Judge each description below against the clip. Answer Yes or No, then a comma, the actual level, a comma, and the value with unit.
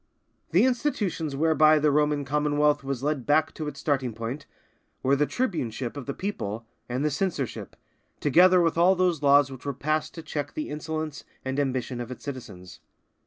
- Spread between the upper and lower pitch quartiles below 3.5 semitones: Yes, average, 2.9 semitones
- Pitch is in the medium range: Yes, medium, 145 Hz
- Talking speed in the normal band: Yes, average, 175 wpm